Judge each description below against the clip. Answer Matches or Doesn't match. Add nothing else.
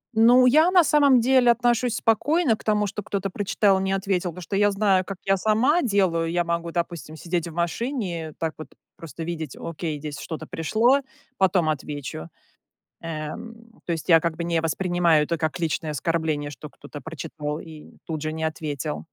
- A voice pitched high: Doesn't match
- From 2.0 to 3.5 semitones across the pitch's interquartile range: Doesn't match